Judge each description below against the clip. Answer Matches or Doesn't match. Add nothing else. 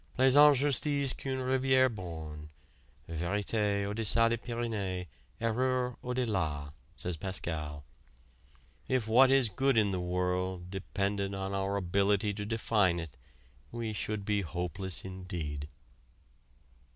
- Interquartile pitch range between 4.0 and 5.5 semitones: Matches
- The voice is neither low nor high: Doesn't match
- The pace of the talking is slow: Matches